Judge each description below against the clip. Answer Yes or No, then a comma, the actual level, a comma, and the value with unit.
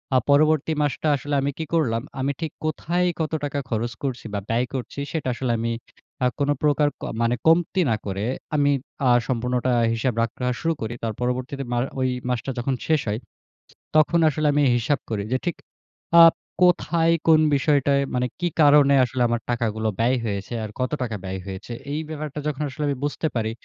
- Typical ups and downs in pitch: Yes, average, 4.2 semitones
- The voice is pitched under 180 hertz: Yes, low, 135 Hz